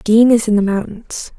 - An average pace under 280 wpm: Yes, fast, 215 wpm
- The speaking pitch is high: Yes, high, 215 Hz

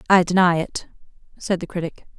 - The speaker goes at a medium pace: Yes, average, 165 wpm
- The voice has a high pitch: No, medium, 175 Hz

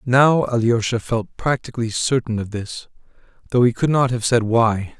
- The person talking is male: Yes, male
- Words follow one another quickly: No, average, 170 wpm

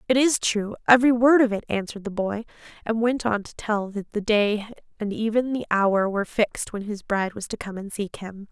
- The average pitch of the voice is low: No, high, 215 Hz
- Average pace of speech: No, fast, 225 wpm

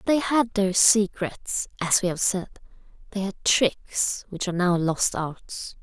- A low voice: No, high, 195 Hz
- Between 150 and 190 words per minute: Yes, average, 165 wpm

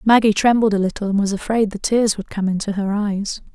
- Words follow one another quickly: Yes, fast, 235 wpm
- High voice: Yes, high, 205 Hz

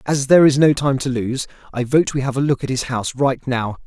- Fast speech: Yes, fast, 280 wpm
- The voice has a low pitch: Yes, low, 130 Hz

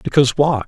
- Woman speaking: No, male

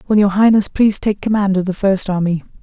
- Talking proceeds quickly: Yes, fast, 230 wpm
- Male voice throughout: No, female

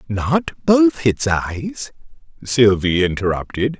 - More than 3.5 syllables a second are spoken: No, 3.3 syllables/s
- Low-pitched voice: Yes, low, 125 Hz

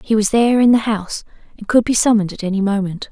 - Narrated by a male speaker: No, female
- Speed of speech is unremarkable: No, fast, 230 wpm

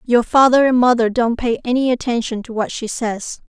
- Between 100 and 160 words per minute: No, fast, 205 wpm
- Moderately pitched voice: No, high, 240 Hz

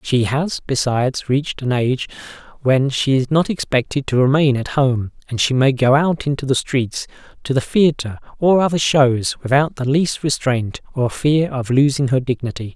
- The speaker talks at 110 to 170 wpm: No, average, 185 wpm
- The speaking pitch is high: No, low, 135 Hz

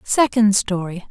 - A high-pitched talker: Yes, high, 205 Hz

